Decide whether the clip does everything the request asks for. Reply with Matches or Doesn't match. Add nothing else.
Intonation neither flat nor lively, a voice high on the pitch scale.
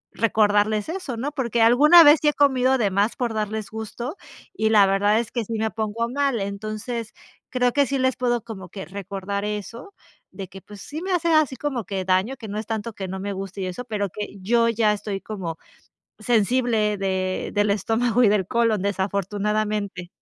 Matches